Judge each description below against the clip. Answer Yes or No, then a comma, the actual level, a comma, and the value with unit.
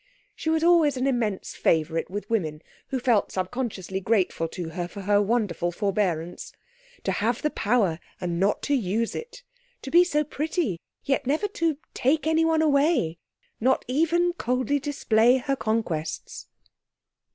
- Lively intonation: Yes, wide, 7.8 semitones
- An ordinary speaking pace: Yes, average, 150 wpm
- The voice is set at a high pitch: Yes, high, 235 Hz